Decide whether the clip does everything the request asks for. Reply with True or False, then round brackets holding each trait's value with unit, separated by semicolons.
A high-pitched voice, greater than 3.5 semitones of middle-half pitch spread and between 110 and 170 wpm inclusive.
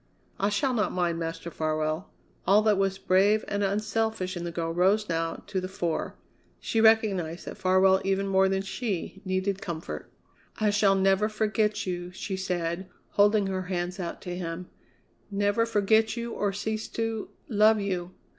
False (195 Hz; 2.7 semitones; 165 wpm)